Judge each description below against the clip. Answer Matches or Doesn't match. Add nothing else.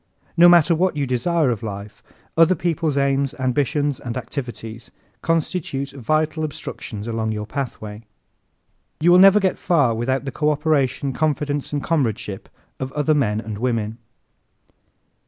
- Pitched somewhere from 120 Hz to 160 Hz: Matches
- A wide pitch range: Doesn't match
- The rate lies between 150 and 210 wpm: Doesn't match